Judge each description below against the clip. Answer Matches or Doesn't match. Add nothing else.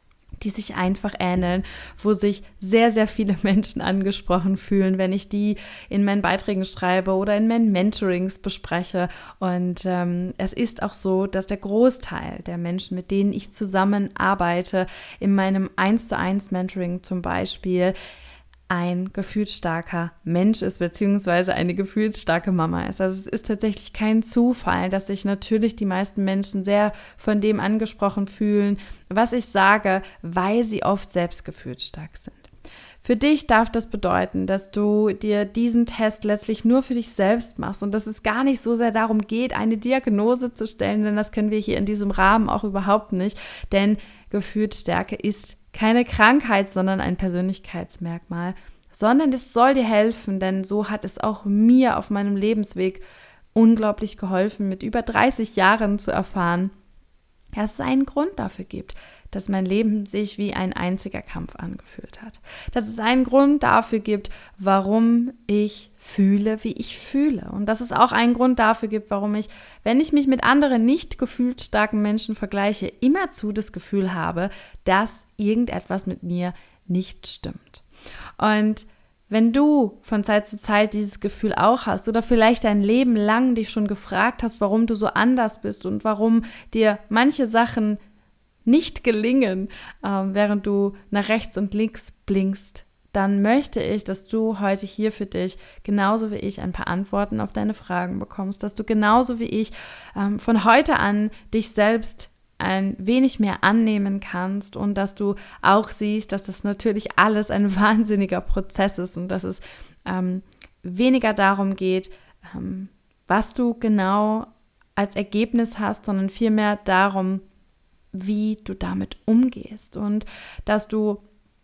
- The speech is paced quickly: Doesn't match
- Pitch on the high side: Matches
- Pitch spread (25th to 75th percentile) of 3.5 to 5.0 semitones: Doesn't match